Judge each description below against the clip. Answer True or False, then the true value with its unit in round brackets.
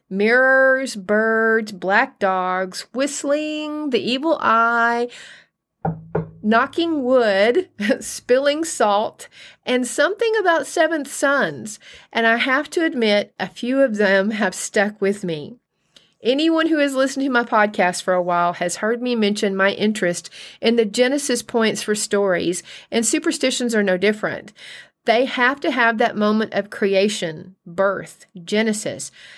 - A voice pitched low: False (225 Hz)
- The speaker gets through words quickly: False (135 wpm)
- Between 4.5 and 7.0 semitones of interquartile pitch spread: True (5.0 semitones)